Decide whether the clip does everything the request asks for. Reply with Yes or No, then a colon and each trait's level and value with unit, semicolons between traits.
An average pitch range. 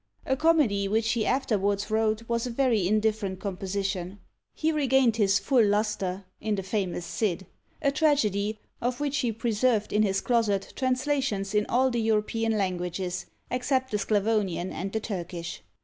Yes: average, 3.9 semitones